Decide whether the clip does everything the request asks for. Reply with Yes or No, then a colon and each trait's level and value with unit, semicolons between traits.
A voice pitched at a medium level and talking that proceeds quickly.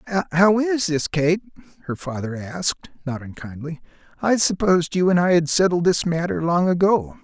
No: medium, 165 Hz; average, 165 wpm